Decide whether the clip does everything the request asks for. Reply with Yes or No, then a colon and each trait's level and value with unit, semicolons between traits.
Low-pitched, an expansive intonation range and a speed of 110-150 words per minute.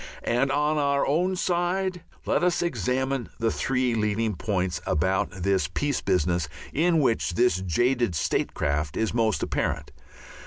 Yes: low, 120 Hz; wide, 7.5 semitones; average, 140 wpm